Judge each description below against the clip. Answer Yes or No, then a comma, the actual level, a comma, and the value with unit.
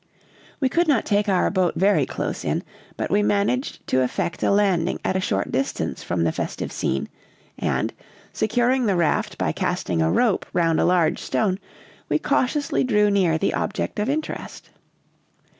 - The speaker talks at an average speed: Yes, average, 170 wpm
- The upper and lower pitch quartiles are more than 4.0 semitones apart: Yes, average, 4.9 semitones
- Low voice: No, high, 200 Hz